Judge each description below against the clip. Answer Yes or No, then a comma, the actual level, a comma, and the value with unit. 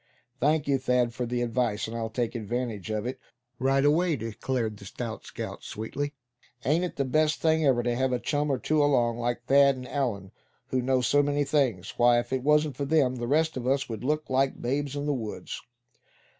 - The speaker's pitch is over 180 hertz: No, low, 130 Hz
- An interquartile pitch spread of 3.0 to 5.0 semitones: Yes, average, 3.3 semitones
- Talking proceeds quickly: Yes, fast, 215 wpm